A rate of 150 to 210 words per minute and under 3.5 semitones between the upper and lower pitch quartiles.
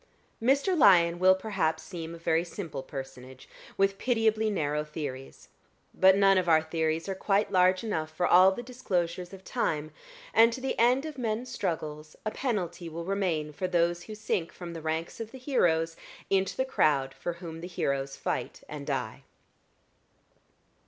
No: average, 170 wpm; average, 4.7 semitones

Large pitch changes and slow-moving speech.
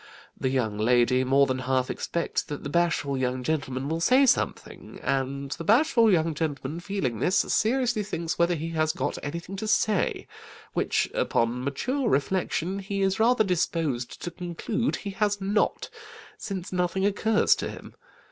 No: wide, 6.6 semitones; average, 160 wpm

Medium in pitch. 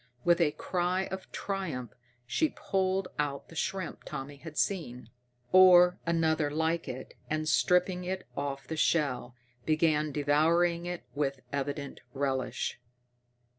Yes: medium, 160 Hz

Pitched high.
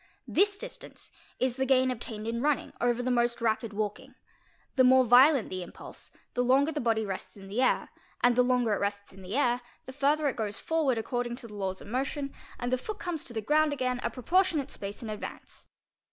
Yes: high, 245 Hz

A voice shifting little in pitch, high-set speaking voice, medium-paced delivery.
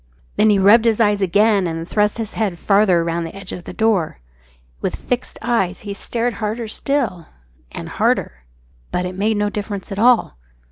No: average, 3.5 semitones; high, 205 Hz; average, 185 wpm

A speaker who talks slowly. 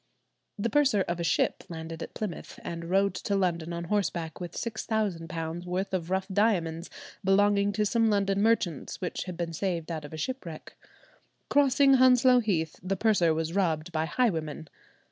No: average, 165 wpm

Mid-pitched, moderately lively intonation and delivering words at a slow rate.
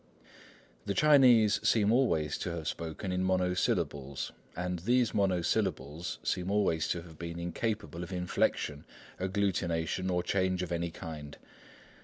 No: very low, 90 Hz; average, 3.1 semitones; slow, 130 wpm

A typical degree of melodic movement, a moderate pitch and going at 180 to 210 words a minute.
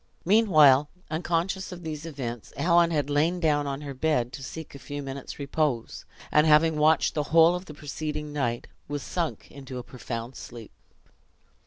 No: average, 3.0 semitones; medium, 150 Hz; average, 170 wpm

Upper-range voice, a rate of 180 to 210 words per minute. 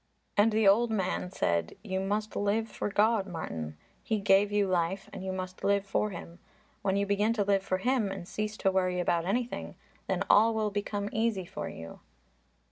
Yes: high, 200 Hz; average, 195 wpm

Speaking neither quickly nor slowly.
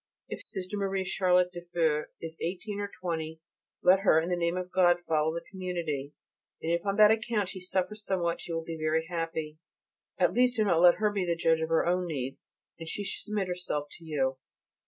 No: fast, 215 wpm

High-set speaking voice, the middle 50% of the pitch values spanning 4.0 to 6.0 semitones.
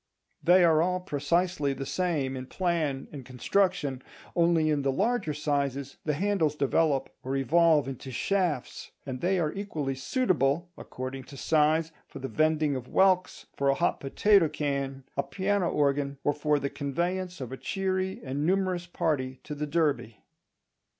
No: medium, 150 Hz; average, 4.4 semitones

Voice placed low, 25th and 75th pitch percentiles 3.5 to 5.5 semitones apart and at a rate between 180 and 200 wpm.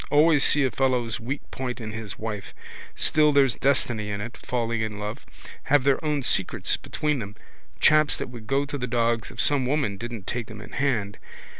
Yes: low, 125 Hz; average, 4.0 semitones; average, 195 wpm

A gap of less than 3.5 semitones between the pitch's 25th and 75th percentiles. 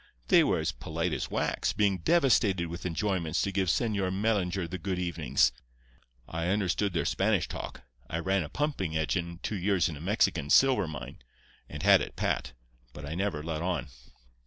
No: average, 3.9 semitones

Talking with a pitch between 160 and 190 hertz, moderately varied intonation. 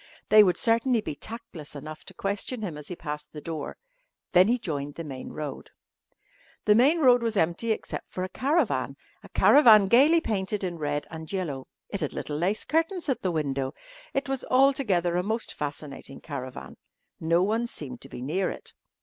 No: medium, 185 Hz; wide, 7.4 semitones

